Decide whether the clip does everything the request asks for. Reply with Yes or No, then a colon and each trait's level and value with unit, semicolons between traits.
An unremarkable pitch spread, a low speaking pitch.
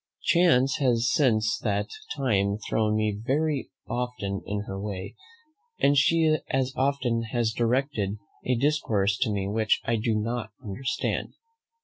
Yes: average, 4.3 semitones; low, 115 Hz